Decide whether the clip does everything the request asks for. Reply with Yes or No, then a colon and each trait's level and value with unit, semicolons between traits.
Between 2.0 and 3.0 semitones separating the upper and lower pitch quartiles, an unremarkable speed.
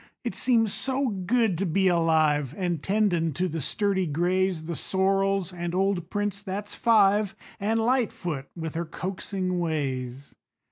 No: average, 3.5 semitones; average, 145 wpm